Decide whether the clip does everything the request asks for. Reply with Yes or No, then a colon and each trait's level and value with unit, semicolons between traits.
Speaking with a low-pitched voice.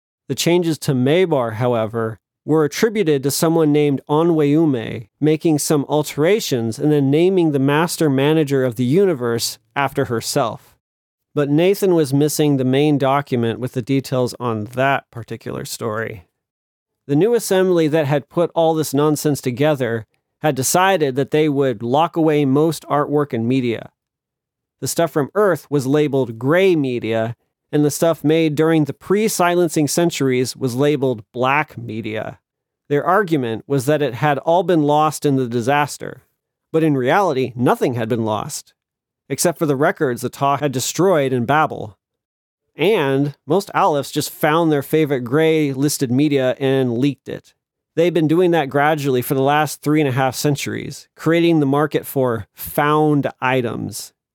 No: medium, 145 Hz